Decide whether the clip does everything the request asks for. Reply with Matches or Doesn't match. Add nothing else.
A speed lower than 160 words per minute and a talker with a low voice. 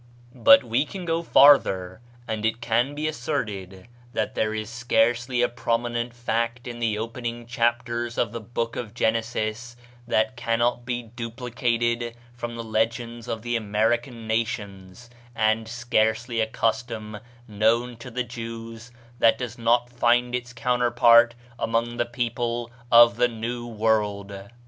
Matches